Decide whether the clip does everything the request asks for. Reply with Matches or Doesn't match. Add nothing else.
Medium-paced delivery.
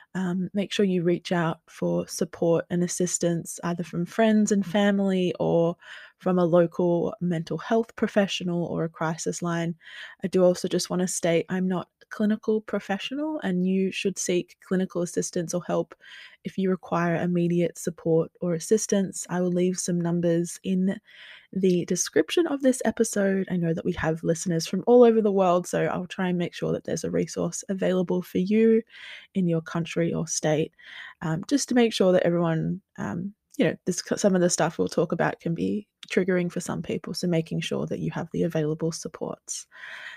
Matches